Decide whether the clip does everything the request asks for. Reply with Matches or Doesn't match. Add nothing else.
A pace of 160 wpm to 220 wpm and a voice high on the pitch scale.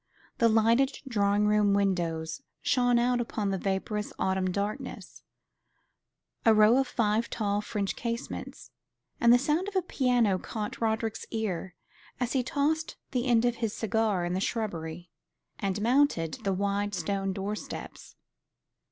Doesn't match